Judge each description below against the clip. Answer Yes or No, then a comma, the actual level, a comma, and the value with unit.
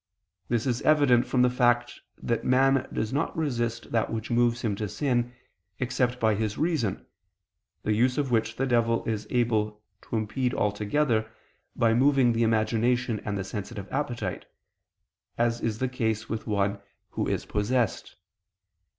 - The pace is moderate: Yes, average, 155 wpm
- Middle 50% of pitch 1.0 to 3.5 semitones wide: Yes, narrow, 2.5 semitones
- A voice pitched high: No, low, 120 Hz